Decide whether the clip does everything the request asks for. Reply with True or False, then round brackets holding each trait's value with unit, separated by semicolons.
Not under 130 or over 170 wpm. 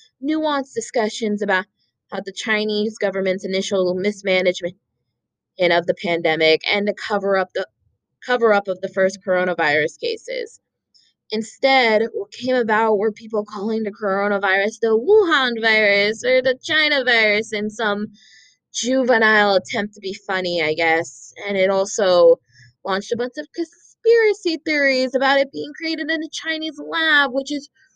True (150 wpm)